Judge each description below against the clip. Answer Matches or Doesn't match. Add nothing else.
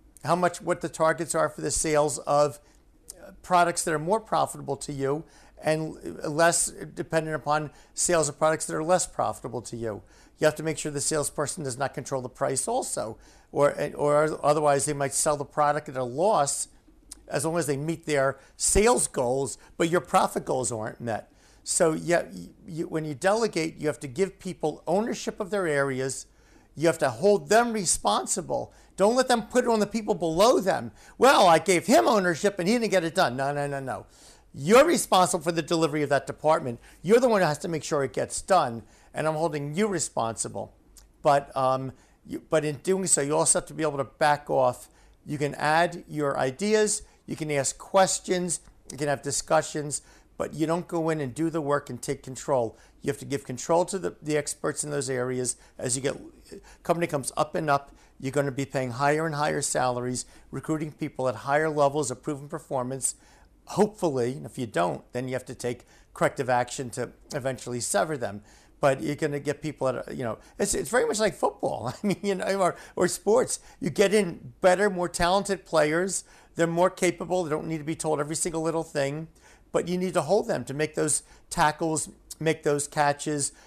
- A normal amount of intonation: Matches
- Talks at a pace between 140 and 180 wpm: Doesn't match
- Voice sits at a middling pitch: Matches